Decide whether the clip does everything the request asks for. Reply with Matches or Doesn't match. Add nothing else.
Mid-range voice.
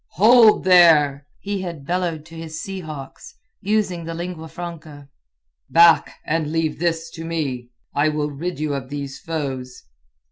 Matches